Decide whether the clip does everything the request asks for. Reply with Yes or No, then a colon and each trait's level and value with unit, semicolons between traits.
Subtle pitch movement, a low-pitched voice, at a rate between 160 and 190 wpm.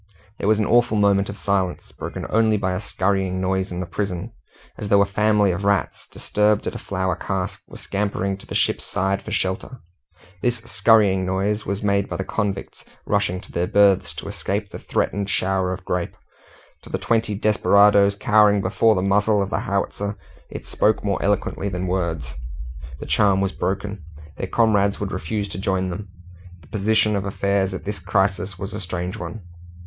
Yes: narrow, 1.7 semitones; low, 100 Hz; average, 185 wpm